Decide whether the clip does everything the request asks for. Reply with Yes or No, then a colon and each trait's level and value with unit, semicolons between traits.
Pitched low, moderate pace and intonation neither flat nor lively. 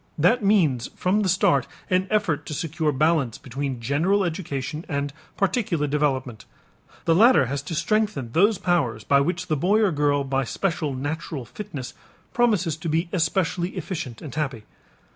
No: medium, 155 Hz; average, 160 wpm; average, 4.8 semitones